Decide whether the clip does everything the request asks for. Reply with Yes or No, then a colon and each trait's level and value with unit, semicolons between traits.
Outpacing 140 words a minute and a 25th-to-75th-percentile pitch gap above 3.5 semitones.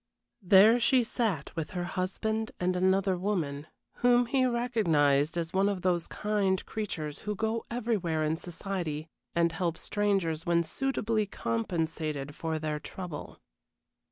No: slow, 135 wpm; average, 4.7 semitones